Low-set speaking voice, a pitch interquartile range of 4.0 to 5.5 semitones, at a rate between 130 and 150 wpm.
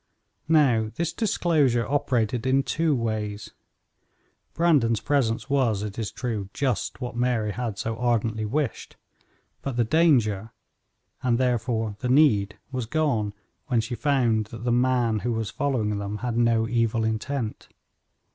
No: low, 120 Hz; average, 3.2 semitones; average, 140 wpm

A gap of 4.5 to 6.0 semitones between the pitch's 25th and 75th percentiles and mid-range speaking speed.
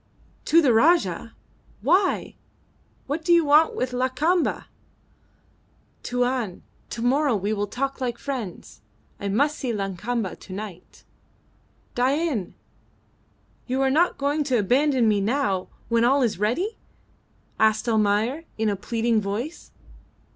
No: average, 5.1 semitones; slow, 125 wpm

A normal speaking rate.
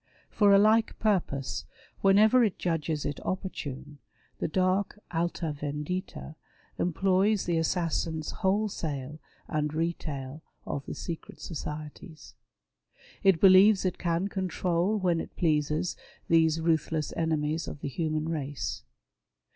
No: slow, 115 wpm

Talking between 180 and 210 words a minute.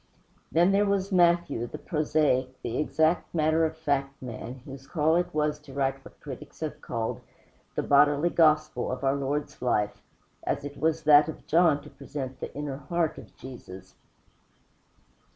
No: average, 165 wpm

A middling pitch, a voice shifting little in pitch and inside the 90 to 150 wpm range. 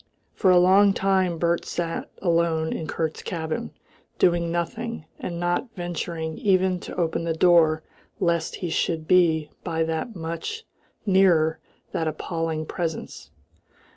Yes: medium, 170 Hz; narrow, 2.2 semitones; slow, 135 wpm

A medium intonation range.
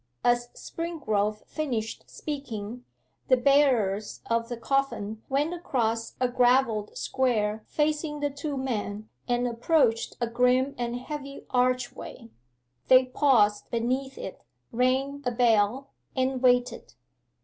Yes: average, 3.2 semitones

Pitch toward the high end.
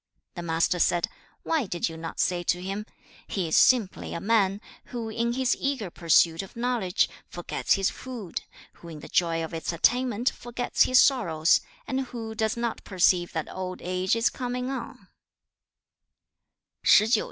Yes: high, 195 Hz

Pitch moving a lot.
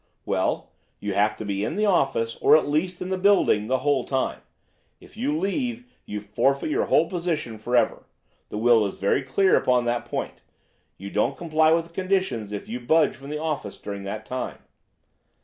Yes: wide, 7.4 semitones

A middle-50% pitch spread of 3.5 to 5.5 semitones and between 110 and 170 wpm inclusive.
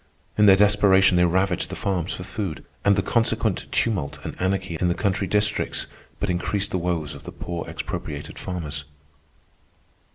No: narrow, 2.6 semitones; average, 165 wpm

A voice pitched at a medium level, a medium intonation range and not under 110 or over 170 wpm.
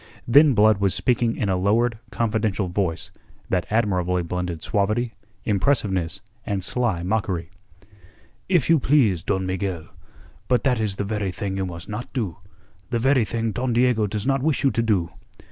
No: low, 105 Hz; average, 4.3 semitones; average, 165 wpm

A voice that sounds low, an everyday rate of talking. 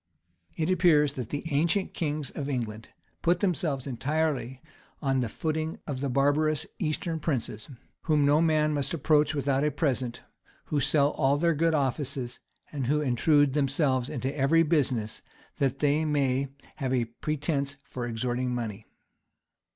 No: medium, 145 Hz; average, 150 wpm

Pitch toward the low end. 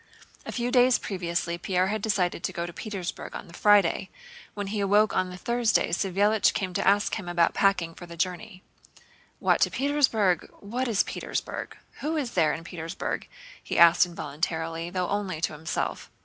No: medium, 185 Hz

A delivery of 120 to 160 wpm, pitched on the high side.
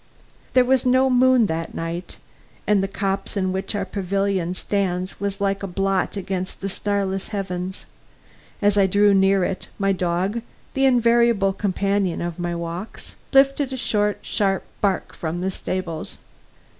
Yes: average, 155 wpm; high, 195 Hz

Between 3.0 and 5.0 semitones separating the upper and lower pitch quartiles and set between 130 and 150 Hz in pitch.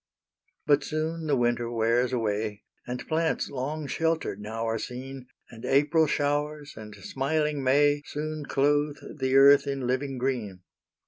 Yes: average, 3.5 semitones; low, 135 Hz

